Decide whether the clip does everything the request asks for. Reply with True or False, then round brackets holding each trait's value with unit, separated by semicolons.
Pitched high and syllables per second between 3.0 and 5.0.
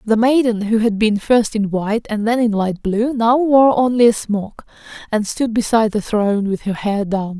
True (220 Hz; 4.9 syllables/s)